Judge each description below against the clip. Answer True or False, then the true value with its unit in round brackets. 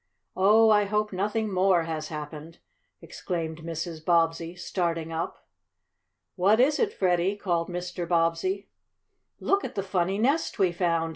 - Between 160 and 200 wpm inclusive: False (140 wpm)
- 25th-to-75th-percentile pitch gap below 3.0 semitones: False (3.3 semitones)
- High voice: False (180 Hz)